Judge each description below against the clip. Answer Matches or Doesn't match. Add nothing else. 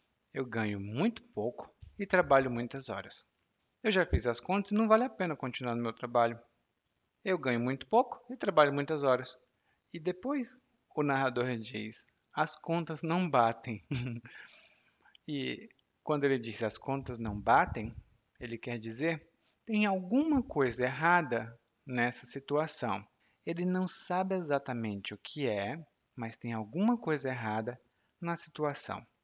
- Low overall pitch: Matches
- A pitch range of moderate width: Doesn't match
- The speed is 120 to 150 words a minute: Matches